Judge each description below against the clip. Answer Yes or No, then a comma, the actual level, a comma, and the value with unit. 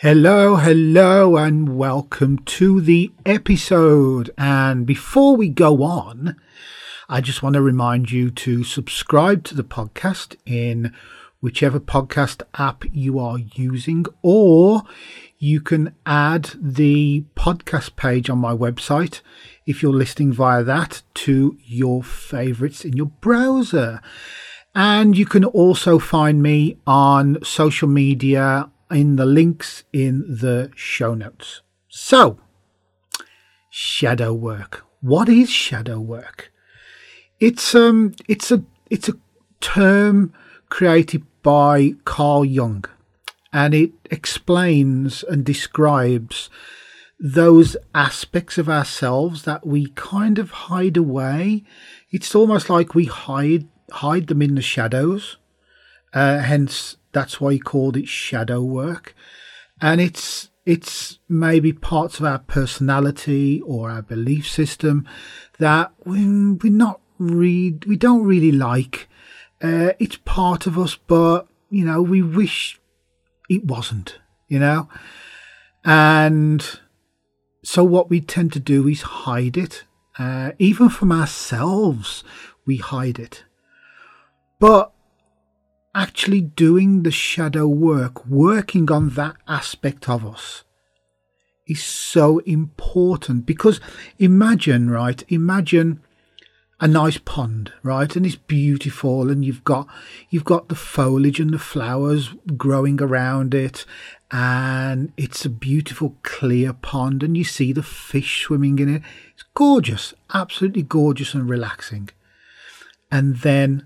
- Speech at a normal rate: No, slow, 120 wpm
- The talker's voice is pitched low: No, medium, 145 Hz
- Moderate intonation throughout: Yes, average, 4.5 semitones